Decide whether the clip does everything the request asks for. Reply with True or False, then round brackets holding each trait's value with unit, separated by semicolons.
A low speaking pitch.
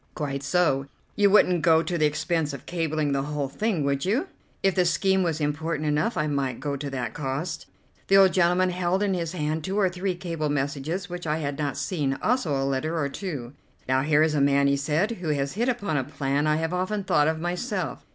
False (155 Hz)